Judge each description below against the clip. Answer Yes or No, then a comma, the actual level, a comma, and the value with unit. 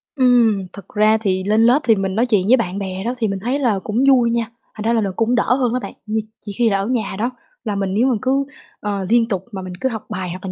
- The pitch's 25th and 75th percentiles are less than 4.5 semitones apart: Yes, average, 3.5 semitones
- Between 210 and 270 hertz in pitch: Yes, high, 220 Hz